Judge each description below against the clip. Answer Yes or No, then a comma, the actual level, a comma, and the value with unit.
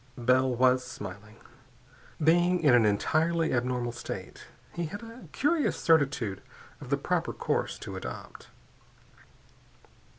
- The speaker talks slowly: Yes, slow, 120 wpm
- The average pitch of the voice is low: Yes, low, 130 Hz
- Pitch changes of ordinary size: No, wide, 5.9 semitones